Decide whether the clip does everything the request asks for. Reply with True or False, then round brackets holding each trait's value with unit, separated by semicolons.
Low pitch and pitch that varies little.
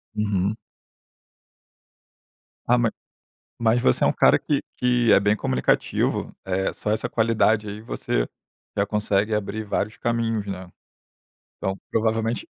True (105 Hz; 2.2 semitones)